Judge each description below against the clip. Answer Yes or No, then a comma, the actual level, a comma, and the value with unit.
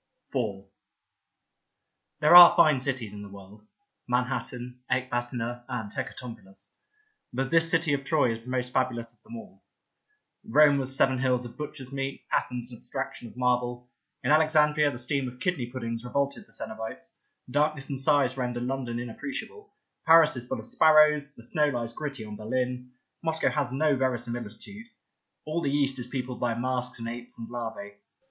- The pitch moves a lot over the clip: No, average, 3.2 semitones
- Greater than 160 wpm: Yes, average, 175 wpm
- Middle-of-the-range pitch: No, low, 125 Hz